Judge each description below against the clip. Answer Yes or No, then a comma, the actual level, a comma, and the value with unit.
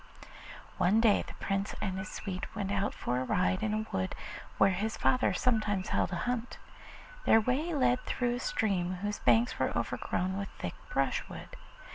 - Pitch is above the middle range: Yes, high, 205 Hz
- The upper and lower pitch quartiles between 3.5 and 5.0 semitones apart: Yes, average, 4.3 semitones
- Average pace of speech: Yes, average, 175 wpm